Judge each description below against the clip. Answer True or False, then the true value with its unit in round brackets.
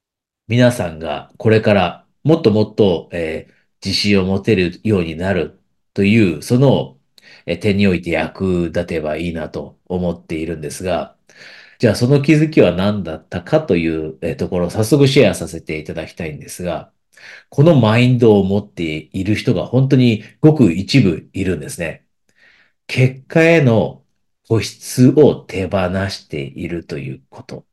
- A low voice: True (100 Hz)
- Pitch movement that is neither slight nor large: False (6.2 semitones)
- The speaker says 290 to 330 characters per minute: True (295 characters per minute)